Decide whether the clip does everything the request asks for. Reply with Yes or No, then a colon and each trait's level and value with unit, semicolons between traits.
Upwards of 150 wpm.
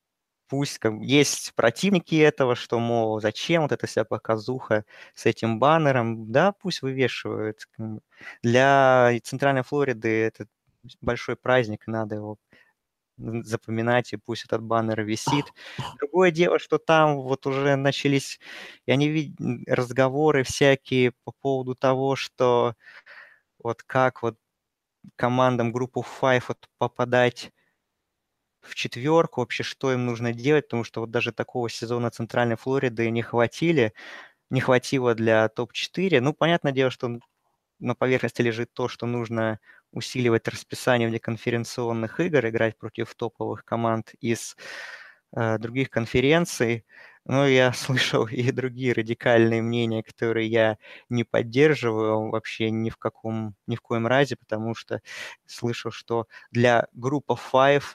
No: average, 130 wpm